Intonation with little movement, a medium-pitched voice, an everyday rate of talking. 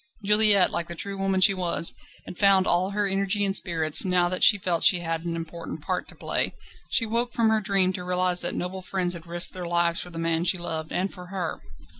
No: narrow, 2.3 semitones; medium, 180 Hz; fast, 240 wpm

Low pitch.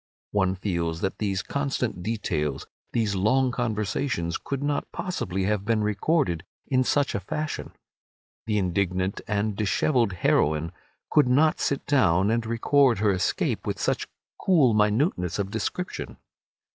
Yes: low, 105 Hz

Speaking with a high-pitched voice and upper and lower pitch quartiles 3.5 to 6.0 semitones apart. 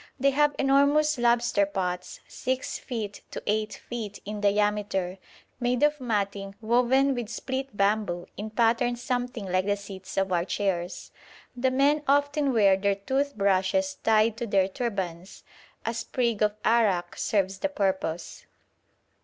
Yes: high, 215 Hz; average, 4.4 semitones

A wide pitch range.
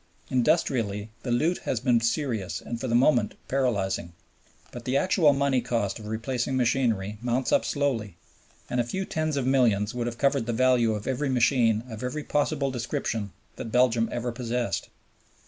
No: average, 2.9 semitones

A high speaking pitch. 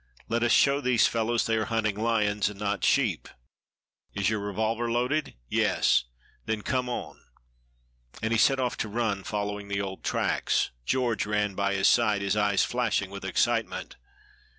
No: low, 110 Hz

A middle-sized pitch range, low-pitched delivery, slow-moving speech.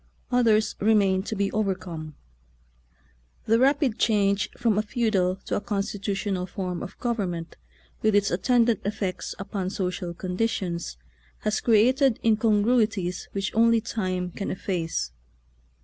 No: average, 3.2 semitones; high, 205 Hz; slow, 130 wpm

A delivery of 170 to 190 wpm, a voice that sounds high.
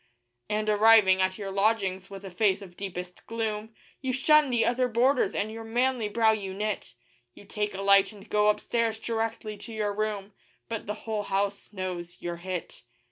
Yes: average, 185 wpm; high, 210 Hz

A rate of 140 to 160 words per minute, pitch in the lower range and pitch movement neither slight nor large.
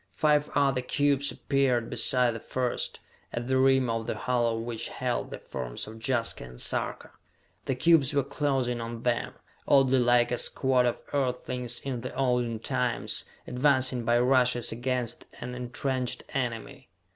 No: average, 155 wpm; low, 125 Hz; narrow, 1.9 semitones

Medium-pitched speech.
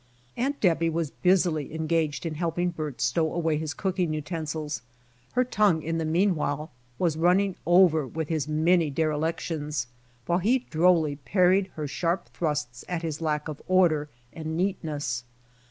Yes: medium, 160 Hz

